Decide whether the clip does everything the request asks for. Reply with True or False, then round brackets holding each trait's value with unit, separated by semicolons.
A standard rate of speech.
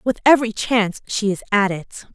True (195 wpm)